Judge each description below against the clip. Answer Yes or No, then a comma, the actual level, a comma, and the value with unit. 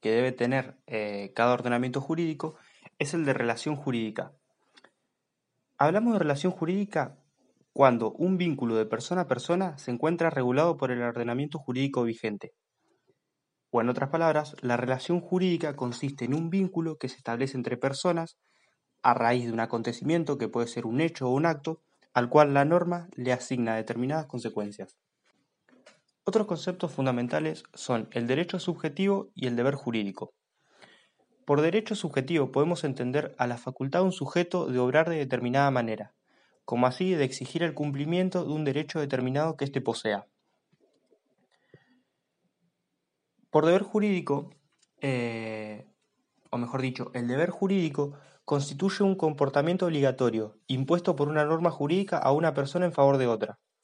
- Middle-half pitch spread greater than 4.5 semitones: Yes, average, 5.2 semitones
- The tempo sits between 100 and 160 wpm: Yes, average, 150 wpm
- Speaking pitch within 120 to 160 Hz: Yes, medium, 140 Hz